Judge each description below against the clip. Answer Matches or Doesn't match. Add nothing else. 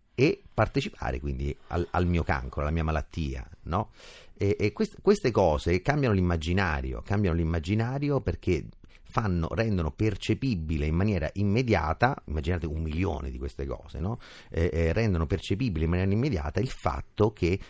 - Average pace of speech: Matches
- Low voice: Matches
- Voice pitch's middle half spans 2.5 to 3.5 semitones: Doesn't match